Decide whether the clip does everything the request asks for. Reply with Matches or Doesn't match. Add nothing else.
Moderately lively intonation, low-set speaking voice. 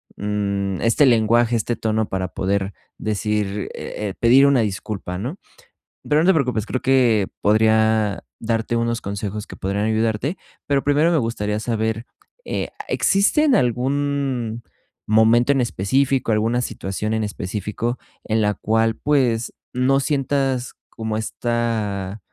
Matches